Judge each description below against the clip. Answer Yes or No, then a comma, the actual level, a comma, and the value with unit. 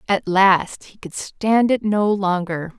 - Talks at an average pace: Yes, average, 170 wpm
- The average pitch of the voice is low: No, high, 195 Hz